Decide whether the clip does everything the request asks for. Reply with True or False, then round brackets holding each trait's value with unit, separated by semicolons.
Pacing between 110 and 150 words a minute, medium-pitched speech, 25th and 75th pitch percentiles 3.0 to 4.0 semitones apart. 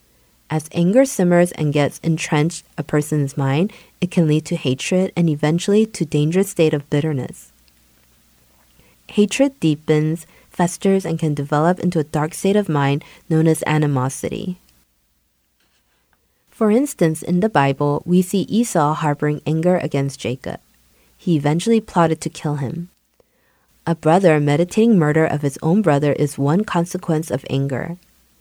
True (140 wpm; 155 Hz; 3.7 semitones)